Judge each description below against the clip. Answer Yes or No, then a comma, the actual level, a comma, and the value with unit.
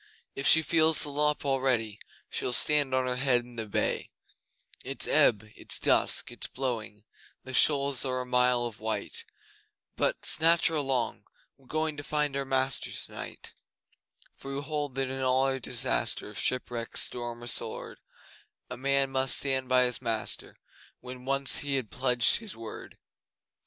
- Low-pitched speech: Yes, low, 130 Hz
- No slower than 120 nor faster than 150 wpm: No, average, 160 wpm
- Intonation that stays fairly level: Yes, narrow, 2.3 semitones